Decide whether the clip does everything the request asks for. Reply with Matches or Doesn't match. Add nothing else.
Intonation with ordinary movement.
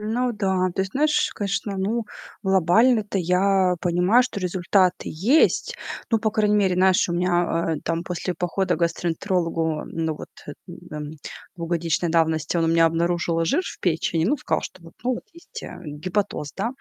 Matches